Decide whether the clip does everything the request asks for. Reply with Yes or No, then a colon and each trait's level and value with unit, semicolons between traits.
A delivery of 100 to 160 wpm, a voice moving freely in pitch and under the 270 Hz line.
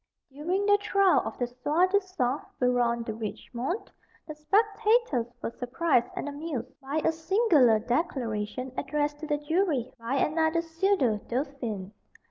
No: slow, 135 wpm; wide, 6.0 semitones; very high, 290 Hz